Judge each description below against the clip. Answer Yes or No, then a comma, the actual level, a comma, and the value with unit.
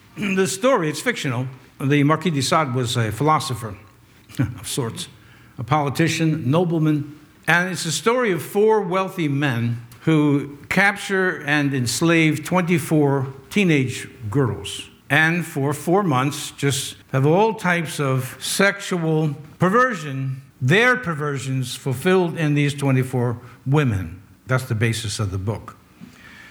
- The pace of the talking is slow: Yes, slow, 125 wpm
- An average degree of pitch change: Yes, average, 4.6 semitones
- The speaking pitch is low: No, medium, 145 Hz